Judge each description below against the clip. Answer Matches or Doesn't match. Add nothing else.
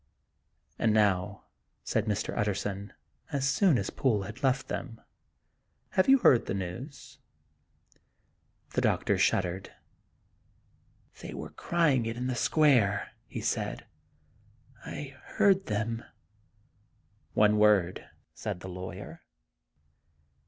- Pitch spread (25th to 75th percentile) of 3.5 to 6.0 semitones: Matches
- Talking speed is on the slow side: Matches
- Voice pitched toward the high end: Doesn't match